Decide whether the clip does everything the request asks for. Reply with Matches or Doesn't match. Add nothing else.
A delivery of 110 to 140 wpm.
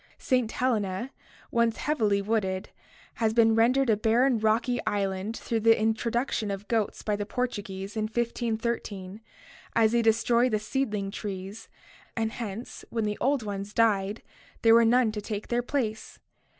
Doesn't match